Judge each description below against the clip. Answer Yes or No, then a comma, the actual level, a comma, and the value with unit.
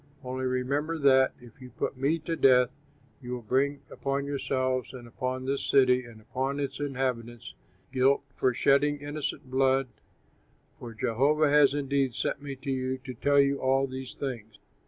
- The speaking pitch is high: No, low, 130 Hz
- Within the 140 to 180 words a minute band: Yes, average, 165 wpm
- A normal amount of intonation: No, narrow, 1.7 semitones